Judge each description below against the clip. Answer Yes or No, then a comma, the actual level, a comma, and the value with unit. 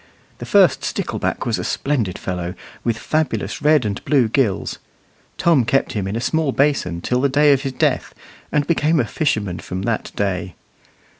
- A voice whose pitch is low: Yes, low, 130 Hz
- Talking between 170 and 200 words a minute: Yes, average, 175 wpm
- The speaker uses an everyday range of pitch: No, wide, 6.4 semitones